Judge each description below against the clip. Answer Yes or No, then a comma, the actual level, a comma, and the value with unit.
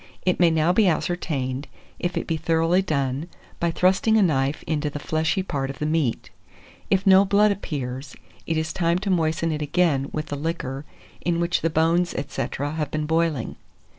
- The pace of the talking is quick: No, average, 185 wpm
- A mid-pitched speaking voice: Yes, medium, 160 Hz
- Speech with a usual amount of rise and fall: Yes, average, 3.1 semitones